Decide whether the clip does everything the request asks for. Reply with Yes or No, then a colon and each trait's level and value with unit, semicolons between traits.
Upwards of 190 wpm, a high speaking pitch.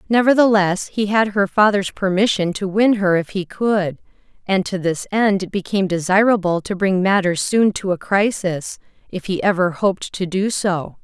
No: average, 180 wpm; high, 195 Hz